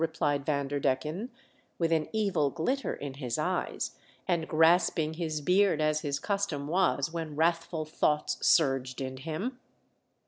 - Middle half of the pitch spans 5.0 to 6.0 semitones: No, average, 3.1 semitones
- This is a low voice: No, medium, 155 Hz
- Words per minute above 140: No, slow, 135 wpm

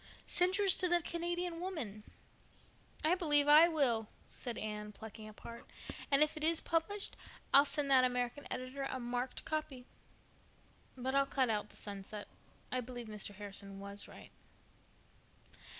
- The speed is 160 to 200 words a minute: No, average, 150 wpm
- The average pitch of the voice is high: Yes, very high, 260 Hz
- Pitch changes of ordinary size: No, wide, 6.3 semitones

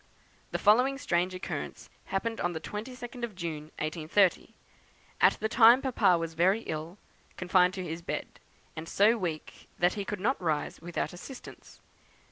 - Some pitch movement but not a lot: Yes, average, 4.9 semitones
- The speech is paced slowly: No, average, 155 wpm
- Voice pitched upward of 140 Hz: Yes, medium, 185 Hz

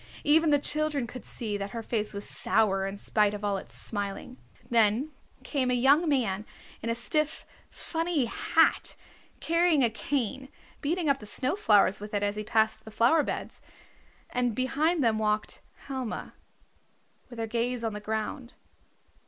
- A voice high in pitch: Yes, high, 235 Hz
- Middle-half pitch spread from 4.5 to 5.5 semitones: Yes, average, 5.0 semitones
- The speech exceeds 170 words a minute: No, average, 165 wpm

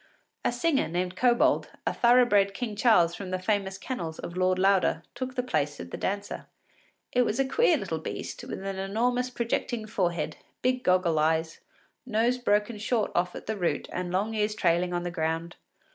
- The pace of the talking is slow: No, average, 190 wpm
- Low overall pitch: No, high, 200 Hz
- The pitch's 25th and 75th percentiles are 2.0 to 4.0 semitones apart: No, average, 5.3 semitones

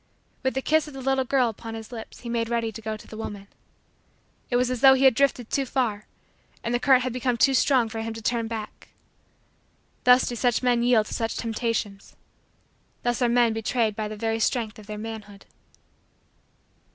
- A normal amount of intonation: No, narrow, 2.2 semitones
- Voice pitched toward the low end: No, high, 235 Hz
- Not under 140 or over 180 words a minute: No, fast, 205 wpm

